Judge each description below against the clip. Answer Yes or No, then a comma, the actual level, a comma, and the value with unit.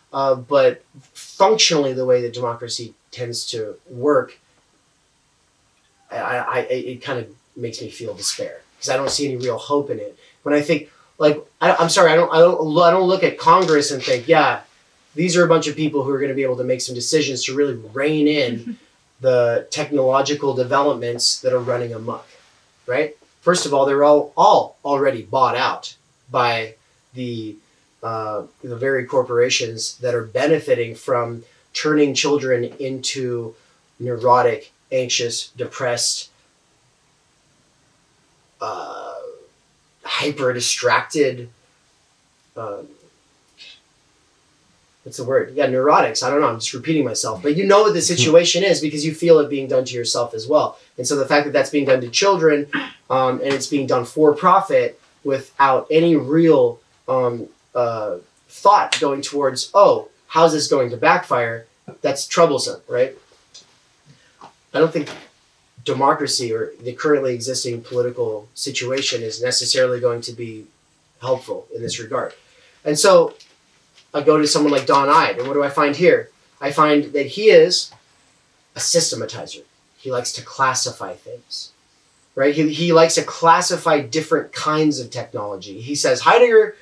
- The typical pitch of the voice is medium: Yes, medium, 145 Hz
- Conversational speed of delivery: Yes, average, 155 wpm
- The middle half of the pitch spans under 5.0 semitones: No, wide, 5.4 semitones